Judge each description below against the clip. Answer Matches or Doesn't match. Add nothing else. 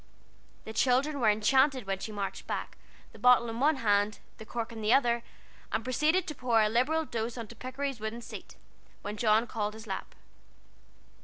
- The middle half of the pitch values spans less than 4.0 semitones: Matches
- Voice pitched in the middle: Doesn't match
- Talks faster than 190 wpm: Doesn't match